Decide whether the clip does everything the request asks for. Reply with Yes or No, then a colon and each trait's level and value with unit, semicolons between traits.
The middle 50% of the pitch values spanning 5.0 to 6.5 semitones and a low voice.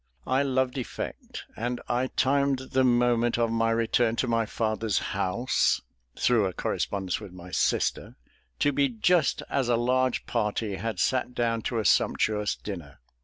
No: average, 3.0 semitones; low, 115 Hz